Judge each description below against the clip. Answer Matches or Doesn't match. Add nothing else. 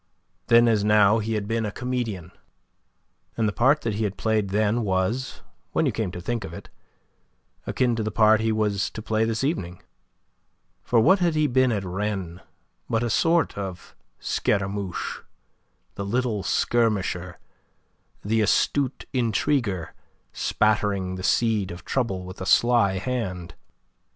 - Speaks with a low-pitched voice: Matches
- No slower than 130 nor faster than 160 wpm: Matches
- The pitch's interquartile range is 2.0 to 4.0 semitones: Matches